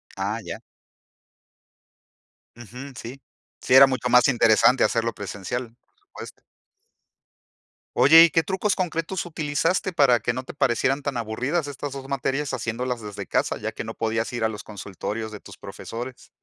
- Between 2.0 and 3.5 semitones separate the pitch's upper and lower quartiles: No, average, 4.0 semitones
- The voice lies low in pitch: Yes, low, 125 Hz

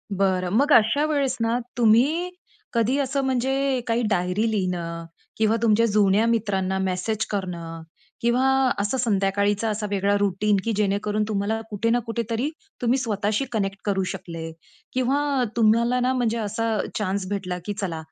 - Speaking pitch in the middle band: No, high, 215 Hz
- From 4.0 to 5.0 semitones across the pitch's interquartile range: No, average, 3.4 semitones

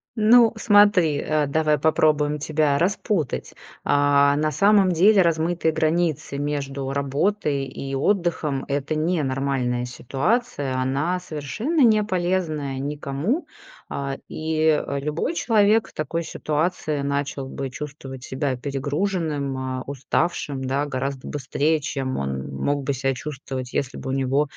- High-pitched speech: No, medium, 145 Hz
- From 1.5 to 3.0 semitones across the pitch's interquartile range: No, average, 3.7 semitones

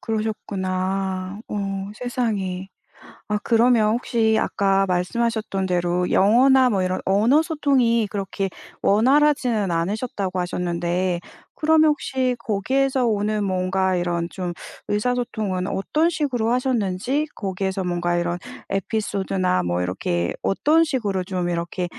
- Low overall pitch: No, high, 200 Hz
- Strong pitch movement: No, average, 4.6 semitones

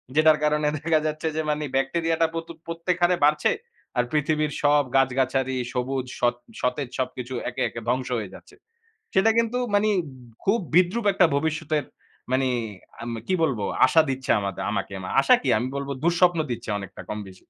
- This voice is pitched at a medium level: Yes, medium, 150 Hz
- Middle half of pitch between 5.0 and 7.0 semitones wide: No, average, 4.4 semitones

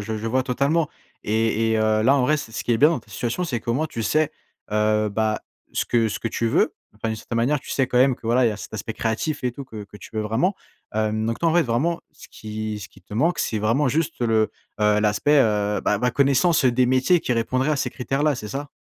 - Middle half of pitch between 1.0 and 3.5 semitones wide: No, average, 4.2 semitones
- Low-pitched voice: Yes, low, 115 Hz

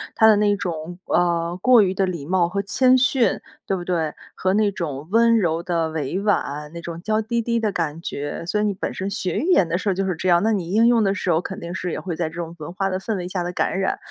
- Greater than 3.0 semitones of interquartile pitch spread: Yes, average, 3.5 semitones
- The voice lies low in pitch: No, medium, 185 Hz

